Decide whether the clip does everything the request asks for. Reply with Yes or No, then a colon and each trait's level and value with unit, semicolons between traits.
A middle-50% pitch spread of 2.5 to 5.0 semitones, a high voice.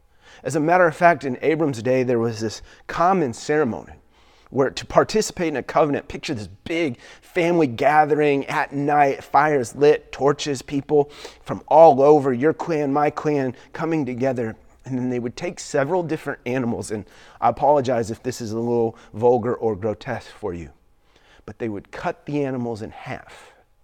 No: average, 4.6 semitones; low, 135 Hz